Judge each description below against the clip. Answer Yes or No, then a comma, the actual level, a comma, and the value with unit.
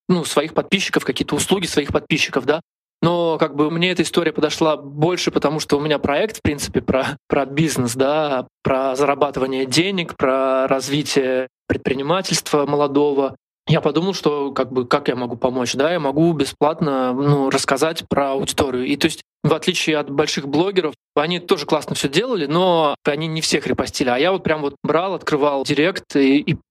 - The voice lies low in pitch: No, medium, 150 Hz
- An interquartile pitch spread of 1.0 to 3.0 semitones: Yes, average, 2.7 semitones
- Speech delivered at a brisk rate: Yes, fast, 180 wpm